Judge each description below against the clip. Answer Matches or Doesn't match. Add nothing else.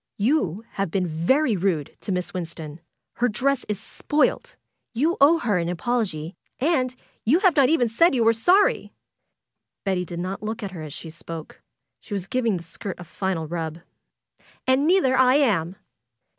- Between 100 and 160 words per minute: Doesn't match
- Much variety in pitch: Matches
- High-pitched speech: Matches